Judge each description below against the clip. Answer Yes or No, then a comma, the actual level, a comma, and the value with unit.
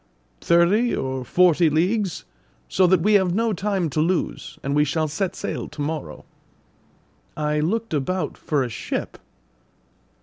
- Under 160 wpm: Yes, average, 145 wpm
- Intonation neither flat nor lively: Yes, average, 4.2 semitones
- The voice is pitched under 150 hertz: No, medium, 170 Hz